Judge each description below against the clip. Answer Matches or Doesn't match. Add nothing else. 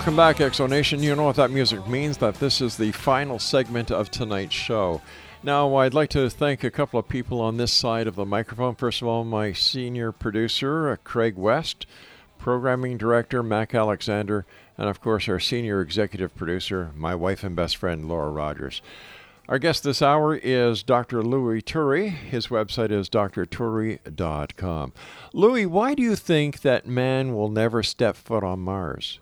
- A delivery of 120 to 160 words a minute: Doesn't match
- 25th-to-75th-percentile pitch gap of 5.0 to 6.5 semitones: Doesn't match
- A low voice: Matches